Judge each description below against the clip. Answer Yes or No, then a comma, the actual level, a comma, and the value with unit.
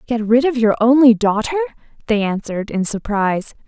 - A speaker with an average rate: Yes, average, 165 wpm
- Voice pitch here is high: Yes, high, 225 Hz